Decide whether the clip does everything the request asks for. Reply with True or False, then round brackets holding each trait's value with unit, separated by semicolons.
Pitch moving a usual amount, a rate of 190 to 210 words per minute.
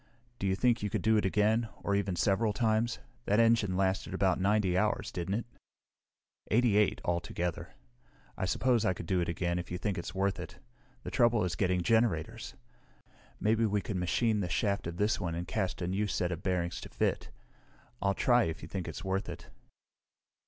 True (3.3 semitones; 195 wpm)